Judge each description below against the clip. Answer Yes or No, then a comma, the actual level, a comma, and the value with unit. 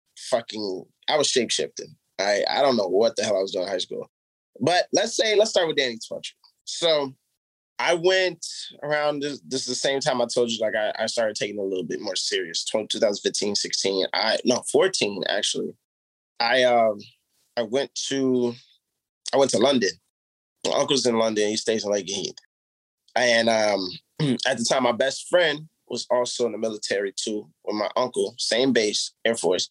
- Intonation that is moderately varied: No, wide, 6.6 semitones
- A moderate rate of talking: Yes, average, 190 wpm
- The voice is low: Yes, low, 125 Hz